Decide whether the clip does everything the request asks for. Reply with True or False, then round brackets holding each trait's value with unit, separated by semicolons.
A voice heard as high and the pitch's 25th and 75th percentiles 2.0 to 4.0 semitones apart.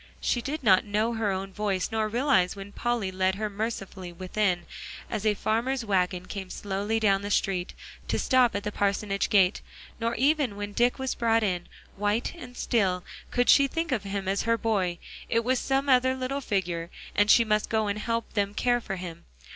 True (210 Hz; 3.5 semitones)